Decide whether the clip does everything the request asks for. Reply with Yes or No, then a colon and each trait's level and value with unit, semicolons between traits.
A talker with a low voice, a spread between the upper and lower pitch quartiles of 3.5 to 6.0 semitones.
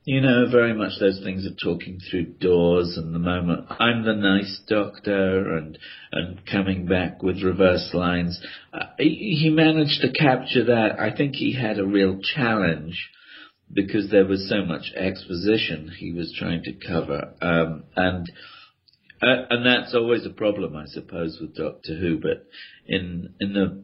Yes: very low, 95 Hz; average, 4.3 semitones